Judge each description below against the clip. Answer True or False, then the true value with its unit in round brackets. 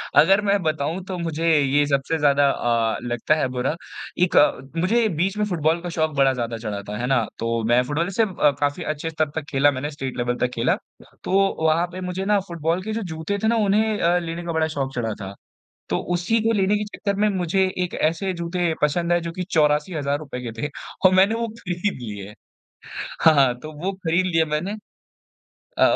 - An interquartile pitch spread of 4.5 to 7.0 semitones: True (4.9 semitones)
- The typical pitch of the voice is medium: True (160 Hz)